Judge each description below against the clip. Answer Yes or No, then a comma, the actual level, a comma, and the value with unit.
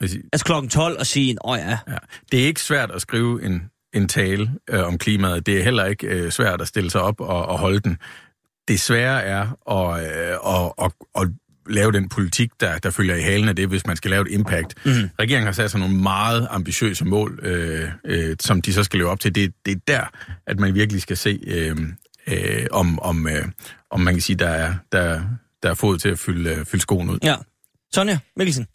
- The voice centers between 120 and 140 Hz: No, low, 100 Hz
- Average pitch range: Yes, average, 4.5 semitones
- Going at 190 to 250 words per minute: No, average, 175 wpm